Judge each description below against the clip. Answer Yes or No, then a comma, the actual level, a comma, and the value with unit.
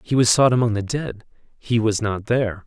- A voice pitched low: Yes, low, 115 Hz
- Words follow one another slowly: No, fast, 225 wpm